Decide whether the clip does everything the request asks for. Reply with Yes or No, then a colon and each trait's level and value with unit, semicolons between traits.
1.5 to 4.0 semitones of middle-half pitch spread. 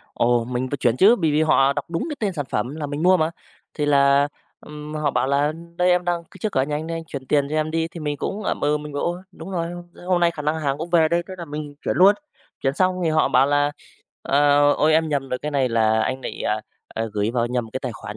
Yes: average, 3.4 semitones